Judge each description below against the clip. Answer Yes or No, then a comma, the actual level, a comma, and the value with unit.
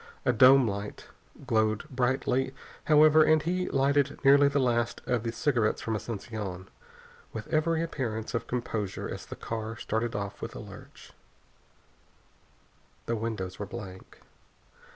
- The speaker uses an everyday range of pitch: Yes, average, 4.2 semitones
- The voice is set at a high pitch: No, low, 120 Hz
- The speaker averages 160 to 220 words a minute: No, slow, 135 wpm